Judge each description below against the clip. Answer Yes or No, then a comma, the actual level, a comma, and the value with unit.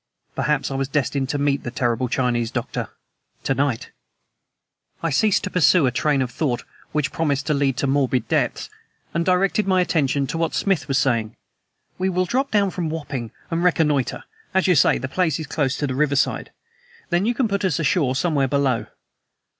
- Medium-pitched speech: Yes, medium, 145 Hz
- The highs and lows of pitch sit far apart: No, average, 4.6 semitones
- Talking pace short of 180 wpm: No, average, 190 wpm